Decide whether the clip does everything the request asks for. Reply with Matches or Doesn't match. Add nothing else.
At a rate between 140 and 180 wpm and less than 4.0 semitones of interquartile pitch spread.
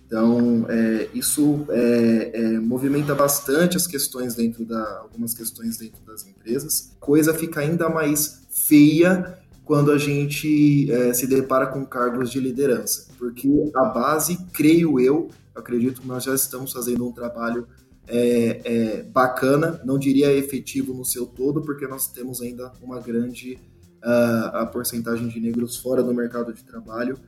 Matches